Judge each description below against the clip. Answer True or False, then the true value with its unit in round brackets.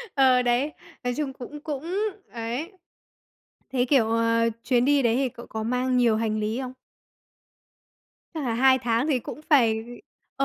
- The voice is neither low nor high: False (250 Hz)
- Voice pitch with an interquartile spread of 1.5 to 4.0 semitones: True (2.8 semitones)